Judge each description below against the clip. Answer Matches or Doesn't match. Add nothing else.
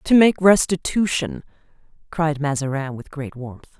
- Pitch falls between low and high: Matches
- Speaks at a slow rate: Matches